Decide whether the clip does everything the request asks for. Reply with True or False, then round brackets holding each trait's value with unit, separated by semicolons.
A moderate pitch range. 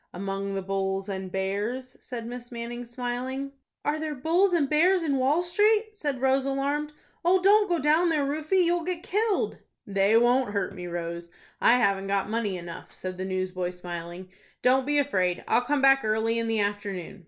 False (7.3 semitones)